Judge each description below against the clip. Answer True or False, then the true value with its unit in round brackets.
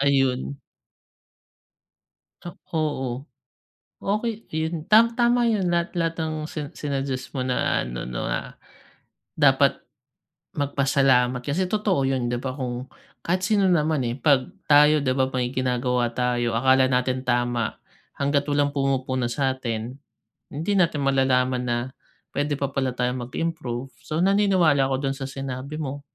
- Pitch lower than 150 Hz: True (135 Hz)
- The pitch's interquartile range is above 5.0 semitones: False (3.7 semitones)